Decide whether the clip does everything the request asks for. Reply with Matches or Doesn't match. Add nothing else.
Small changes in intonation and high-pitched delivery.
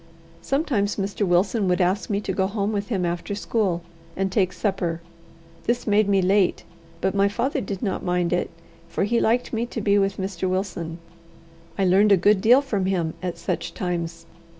Matches